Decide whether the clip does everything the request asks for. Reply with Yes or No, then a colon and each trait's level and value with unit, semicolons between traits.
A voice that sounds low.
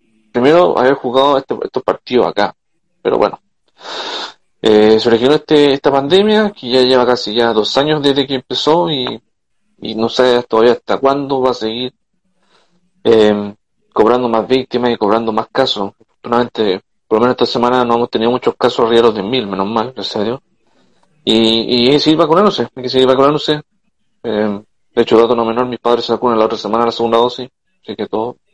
Yes: low, 125 Hz